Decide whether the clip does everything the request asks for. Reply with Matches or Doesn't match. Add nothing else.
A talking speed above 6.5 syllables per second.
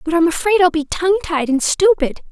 Doesn't match